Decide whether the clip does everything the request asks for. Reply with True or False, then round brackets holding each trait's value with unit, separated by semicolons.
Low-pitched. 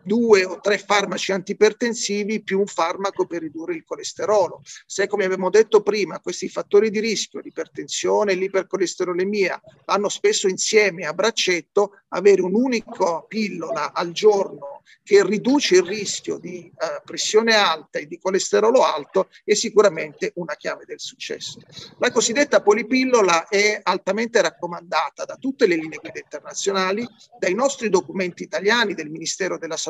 False (205 Hz)